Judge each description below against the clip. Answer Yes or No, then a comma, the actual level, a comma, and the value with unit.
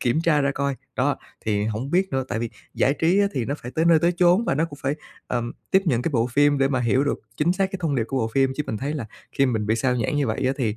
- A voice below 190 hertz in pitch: Yes, low, 135 Hz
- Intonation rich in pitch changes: No, average, 4.6 semitones